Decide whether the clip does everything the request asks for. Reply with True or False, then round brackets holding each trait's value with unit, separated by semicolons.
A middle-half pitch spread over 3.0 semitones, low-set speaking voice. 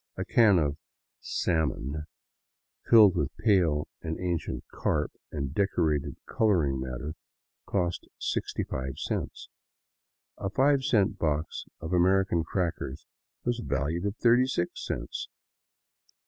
True (5.3 semitones; 85 Hz)